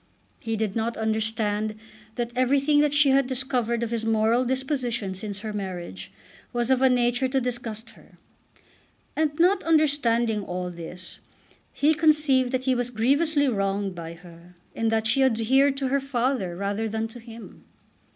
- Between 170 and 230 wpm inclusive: No, average, 160 wpm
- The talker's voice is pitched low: No, high, 235 Hz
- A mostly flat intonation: No, average, 3.7 semitones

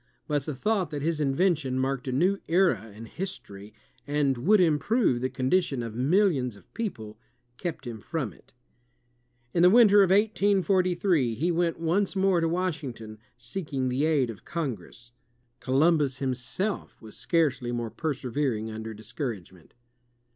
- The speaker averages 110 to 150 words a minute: Yes, average, 145 wpm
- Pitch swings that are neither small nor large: No, wide, 6.7 semitones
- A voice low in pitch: No, medium, 145 Hz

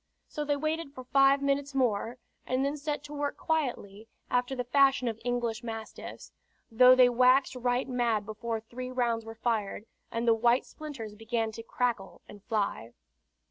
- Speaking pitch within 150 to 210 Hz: No, high, 245 Hz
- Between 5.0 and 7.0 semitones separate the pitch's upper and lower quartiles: No, average, 3.3 semitones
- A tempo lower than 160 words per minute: No, average, 170 wpm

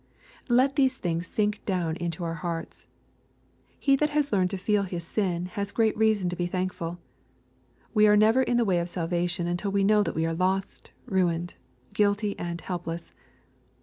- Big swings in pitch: No, average, 3.5 semitones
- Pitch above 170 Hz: Yes, medium, 185 Hz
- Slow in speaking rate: No, average, 180 wpm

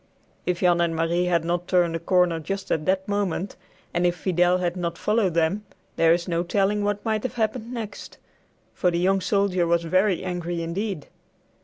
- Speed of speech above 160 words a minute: Yes, average, 190 wpm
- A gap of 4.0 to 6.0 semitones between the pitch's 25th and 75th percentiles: No, narrow, 2.6 semitones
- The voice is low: No, medium, 180 Hz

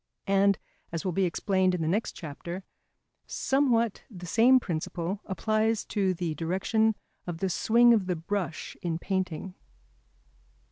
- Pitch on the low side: No, high, 190 Hz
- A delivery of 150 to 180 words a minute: No, average, 140 wpm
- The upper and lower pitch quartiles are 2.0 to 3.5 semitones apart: No, average, 4.0 semitones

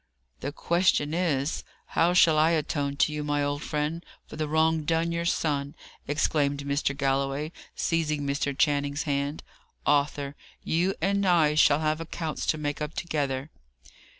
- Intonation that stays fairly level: Yes, narrow, 2.2 semitones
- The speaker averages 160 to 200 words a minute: No, average, 150 wpm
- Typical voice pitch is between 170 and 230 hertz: No, medium, 150 Hz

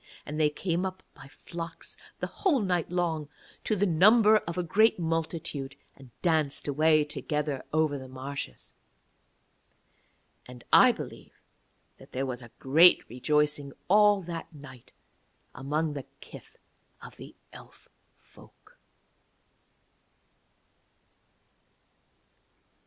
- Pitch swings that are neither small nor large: Yes, average, 3.9 semitones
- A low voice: No, medium, 155 Hz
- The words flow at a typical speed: No, slow, 115 wpm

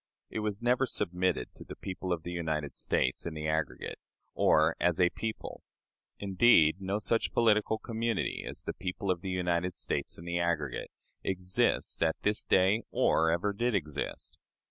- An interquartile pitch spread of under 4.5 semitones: Yes, average, 4.1 semitones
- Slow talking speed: No, average, 165 wpm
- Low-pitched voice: Yes, very low, 90 Hz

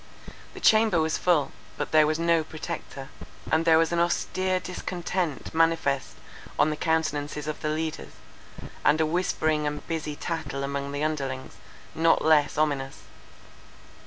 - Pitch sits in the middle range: Yes, medium, 155 Hz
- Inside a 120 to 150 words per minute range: Yes, average, 140 wpm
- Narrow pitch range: Yes, narrow, 2.1 semitones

